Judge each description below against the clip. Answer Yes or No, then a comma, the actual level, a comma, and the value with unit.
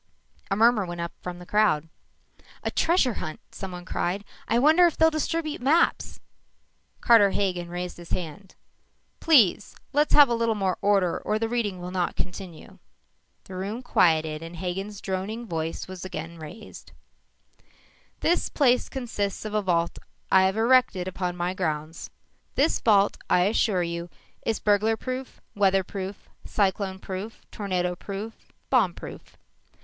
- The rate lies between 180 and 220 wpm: No, average, 155 wpm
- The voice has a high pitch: Yes, high, 195 Hz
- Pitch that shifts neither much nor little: Yes, average, 4.1 semitones